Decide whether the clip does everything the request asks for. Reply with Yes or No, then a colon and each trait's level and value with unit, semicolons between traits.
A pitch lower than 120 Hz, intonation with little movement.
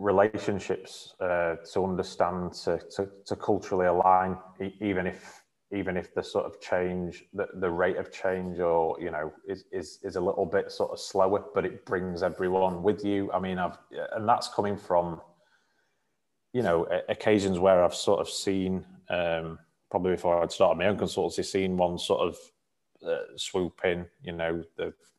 Yes: very low, 95 Hz; narrow, 2.2 semitones